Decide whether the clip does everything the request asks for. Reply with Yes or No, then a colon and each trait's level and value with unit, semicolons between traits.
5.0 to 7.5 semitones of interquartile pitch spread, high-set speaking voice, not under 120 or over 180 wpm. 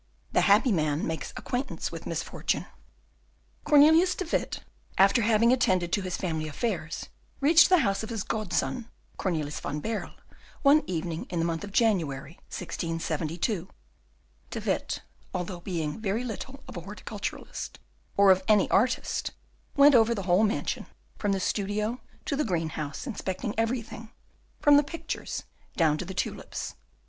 Yes: wide, 5.6 semitones; high, 200 Hz; average, 150 wpm